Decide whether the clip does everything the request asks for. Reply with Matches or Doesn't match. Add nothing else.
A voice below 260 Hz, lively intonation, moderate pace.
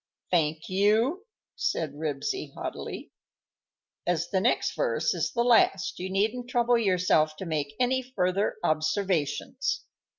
Doesn't match